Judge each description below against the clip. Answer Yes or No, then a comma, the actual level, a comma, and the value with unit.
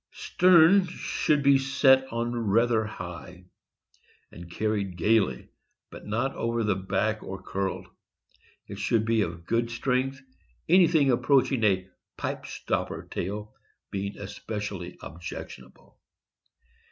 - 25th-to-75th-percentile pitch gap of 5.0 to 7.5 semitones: Yes, wide, 5.5 semitones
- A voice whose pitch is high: No, low, 110 Hz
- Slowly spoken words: Yes, slow, 115 wpm